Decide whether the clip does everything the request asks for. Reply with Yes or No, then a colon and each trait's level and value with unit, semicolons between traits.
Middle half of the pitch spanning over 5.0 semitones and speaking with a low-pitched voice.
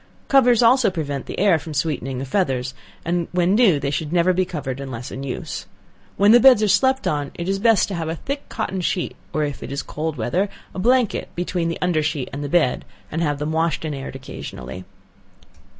No: wide, 5.6 semitones; medium, 165 Hz